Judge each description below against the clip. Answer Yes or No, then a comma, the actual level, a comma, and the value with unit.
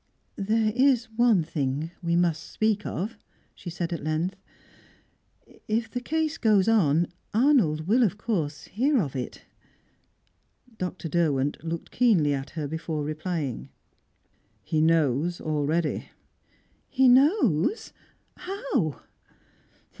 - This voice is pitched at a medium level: Yes, medium, 175 Hz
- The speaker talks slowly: Yes, slow, 115 wpm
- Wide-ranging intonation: Yes, wide, 6.5 semitones